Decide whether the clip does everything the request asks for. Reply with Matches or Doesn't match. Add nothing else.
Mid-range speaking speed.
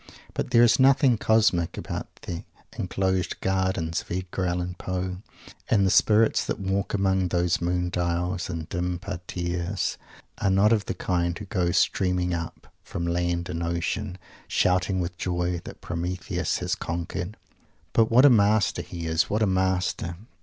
Matches